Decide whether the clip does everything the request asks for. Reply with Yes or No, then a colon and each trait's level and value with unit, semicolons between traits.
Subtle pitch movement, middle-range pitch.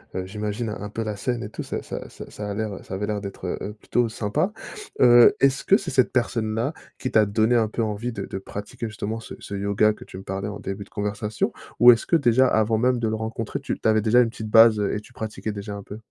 No: narrow, 2.3 semitones; low, 110 Hz